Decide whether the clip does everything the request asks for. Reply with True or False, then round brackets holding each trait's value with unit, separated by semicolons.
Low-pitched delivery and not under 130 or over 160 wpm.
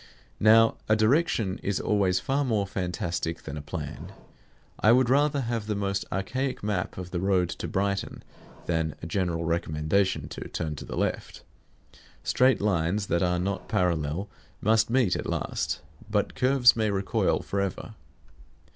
True (100 Hz; 155 wpm)